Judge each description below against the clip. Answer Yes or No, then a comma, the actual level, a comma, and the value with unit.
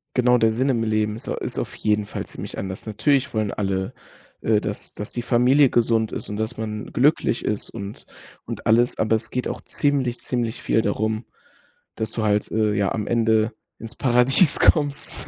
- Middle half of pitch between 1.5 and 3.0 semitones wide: Yes, narrow, 2.5 semitones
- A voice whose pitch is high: No, low, 110 Hz